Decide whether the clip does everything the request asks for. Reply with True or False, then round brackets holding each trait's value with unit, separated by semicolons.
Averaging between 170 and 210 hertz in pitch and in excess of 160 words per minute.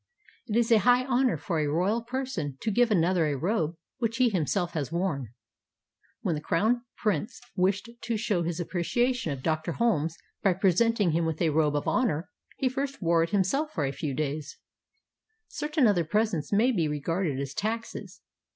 True (185 Hz; 175 wpm)